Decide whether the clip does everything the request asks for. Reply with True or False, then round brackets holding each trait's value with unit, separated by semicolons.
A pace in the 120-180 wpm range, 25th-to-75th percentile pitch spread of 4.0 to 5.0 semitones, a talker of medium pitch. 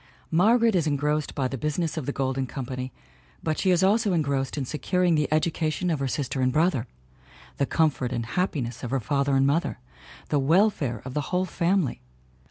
False (190 wpm; 4.4 semitones; 150 Hz)